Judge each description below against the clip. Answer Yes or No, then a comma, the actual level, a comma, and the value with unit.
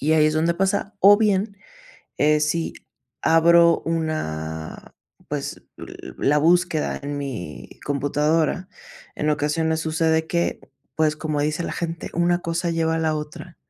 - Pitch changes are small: Yes, narrow, 2.2 semitones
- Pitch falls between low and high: Yes, medium, 160 Hz